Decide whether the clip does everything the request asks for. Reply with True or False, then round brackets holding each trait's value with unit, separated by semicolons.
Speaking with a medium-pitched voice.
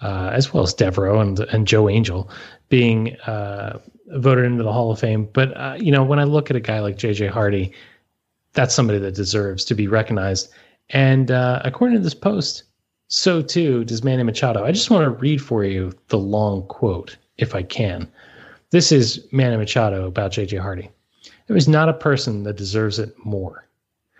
False (110 Hz)